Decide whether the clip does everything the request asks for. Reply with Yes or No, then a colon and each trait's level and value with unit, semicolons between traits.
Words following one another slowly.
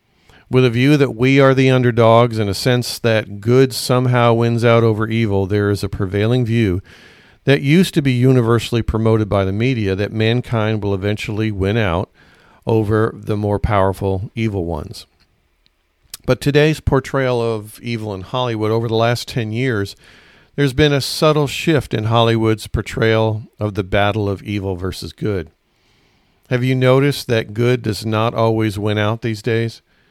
No: average, 165 wpm